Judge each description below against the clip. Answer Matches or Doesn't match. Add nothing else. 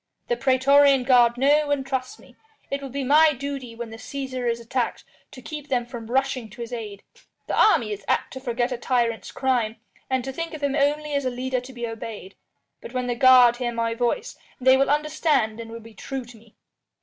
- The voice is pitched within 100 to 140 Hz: Doesn't match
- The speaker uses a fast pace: Matches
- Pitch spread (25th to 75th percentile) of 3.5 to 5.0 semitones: Doesn't match